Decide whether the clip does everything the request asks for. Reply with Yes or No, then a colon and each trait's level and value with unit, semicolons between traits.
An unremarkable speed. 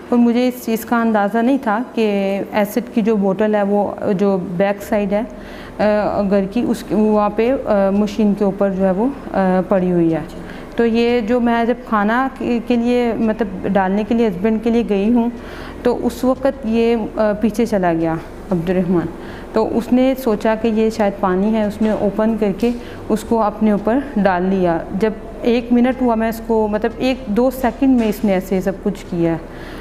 No: fast, 205 wpm